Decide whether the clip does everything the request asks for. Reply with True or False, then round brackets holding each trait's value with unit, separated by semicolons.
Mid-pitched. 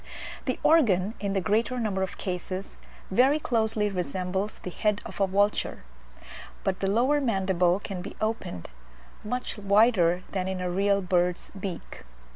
False (195 Hz)